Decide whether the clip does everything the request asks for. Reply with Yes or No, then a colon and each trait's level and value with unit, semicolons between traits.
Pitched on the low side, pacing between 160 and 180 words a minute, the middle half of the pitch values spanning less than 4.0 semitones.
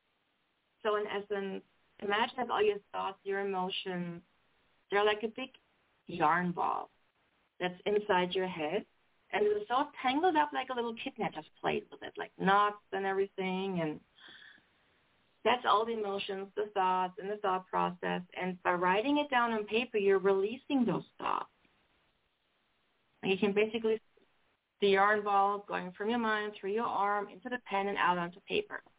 No: high, 200 Hz; average, 170 wpm; average, 3.2 semitones